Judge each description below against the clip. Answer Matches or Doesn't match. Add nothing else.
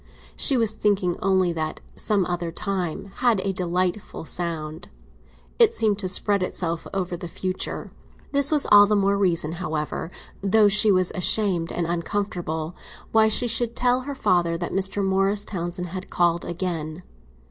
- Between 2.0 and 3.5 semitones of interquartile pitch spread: Matches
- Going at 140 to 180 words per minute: Matches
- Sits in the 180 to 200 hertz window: Matches